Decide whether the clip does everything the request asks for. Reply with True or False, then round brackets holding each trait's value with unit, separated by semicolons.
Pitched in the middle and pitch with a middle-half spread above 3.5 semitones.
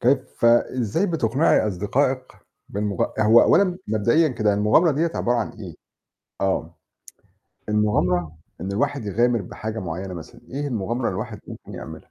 False (110 Hz; 4.7 semitones)